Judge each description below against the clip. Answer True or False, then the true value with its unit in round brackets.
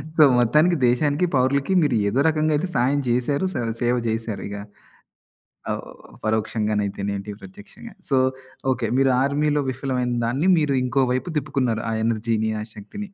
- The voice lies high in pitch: False (130 Hz)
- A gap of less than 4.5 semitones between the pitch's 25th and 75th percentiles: False (4.8 semitones)